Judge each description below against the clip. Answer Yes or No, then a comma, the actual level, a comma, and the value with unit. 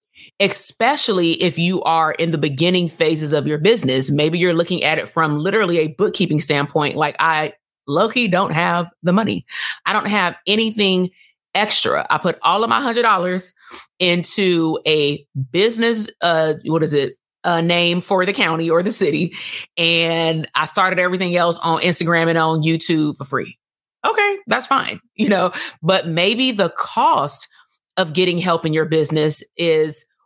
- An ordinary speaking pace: Yes, average, 165 wpm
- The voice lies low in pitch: No, medium, 170 Hz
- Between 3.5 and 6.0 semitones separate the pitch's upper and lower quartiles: No, average, 3.0 semitones